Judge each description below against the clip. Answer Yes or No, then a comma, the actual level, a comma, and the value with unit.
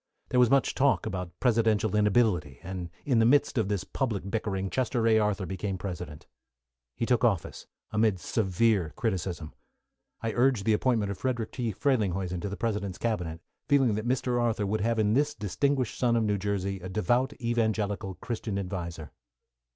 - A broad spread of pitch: No, average, 3.7 semitones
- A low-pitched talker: Yes, low, 105 Hz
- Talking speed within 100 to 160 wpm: No, average, 170 wpm